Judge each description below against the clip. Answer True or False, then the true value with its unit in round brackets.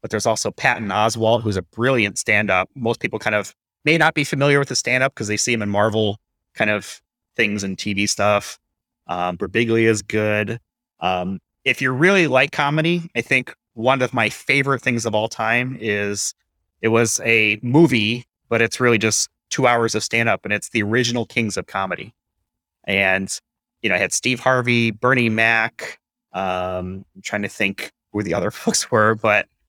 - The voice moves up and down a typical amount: True (3.1 semitones)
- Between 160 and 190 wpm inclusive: True (185 wpm)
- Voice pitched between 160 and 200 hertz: False (115 Hz)